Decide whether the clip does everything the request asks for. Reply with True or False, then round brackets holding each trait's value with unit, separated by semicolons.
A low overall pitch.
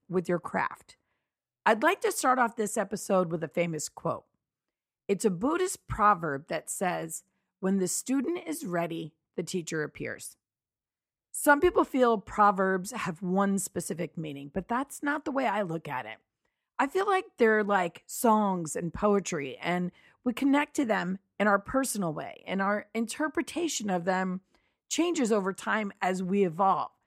False (200 Hz)